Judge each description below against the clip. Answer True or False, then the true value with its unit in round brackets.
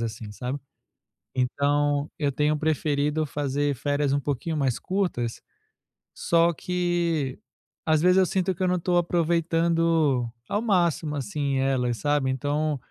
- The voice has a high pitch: False (150 Hz)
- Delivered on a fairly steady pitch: False (3.3 semitones)